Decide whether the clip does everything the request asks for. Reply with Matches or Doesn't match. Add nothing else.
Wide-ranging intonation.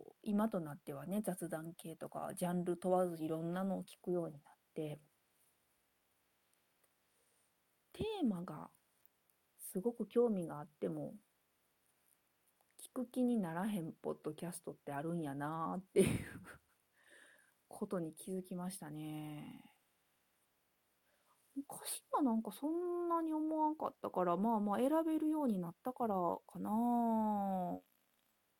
Matches